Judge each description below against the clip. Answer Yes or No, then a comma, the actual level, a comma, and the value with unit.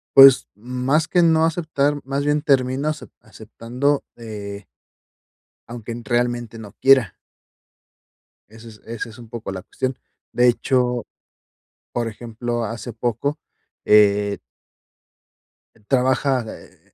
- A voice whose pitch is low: Yes, low, 120 Hz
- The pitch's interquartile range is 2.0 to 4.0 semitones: Yes, average, 3.2 semitones